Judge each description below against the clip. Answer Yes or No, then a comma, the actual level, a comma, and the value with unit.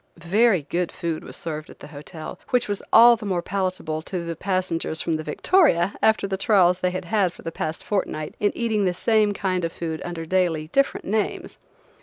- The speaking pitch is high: No, medium, 180 Hz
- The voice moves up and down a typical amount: Yes, average, 3.7 semitones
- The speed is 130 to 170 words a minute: No, average, 200 wpm